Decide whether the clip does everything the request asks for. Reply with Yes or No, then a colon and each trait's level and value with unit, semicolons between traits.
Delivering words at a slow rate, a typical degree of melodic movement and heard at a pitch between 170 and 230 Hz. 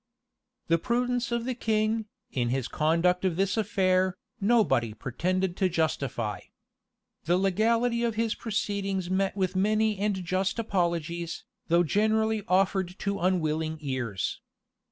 Yes: slow, 130 wpm; average, 4.3 semitones; high, 190 Hz